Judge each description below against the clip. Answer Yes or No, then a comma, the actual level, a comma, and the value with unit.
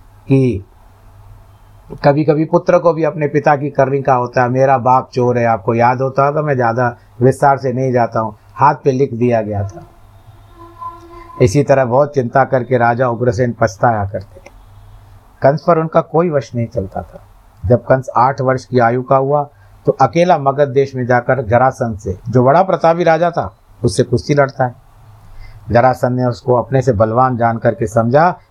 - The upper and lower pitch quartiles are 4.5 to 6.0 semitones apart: No, average, 3.7 semitones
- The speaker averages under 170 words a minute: No, average, 180 wpm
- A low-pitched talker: Yes, low, 125 Hz